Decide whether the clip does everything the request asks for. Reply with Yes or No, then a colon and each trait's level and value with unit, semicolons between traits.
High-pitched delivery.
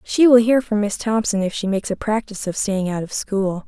Yes: high, 210 Hz